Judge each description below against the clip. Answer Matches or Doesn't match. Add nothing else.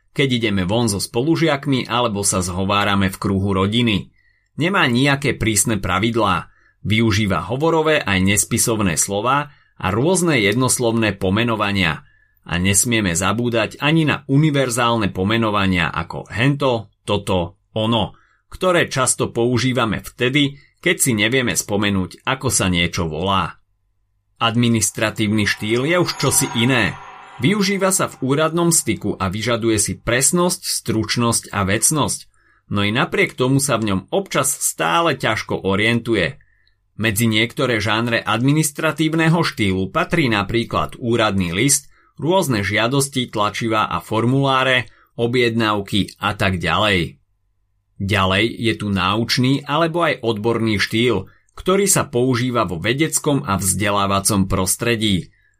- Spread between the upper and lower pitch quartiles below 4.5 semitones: Doesn't match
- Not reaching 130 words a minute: Matches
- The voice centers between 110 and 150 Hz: Matches